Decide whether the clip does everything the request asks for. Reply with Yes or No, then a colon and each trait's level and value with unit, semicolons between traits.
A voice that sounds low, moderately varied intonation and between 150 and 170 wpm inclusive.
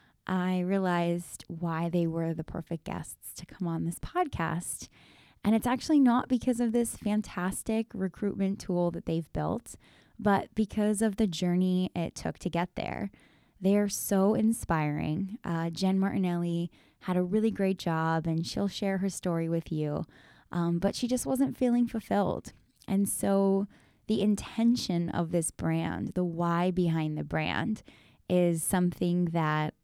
No: medium, 185 Hz; average, 3.5 semitones; average, 155 wpm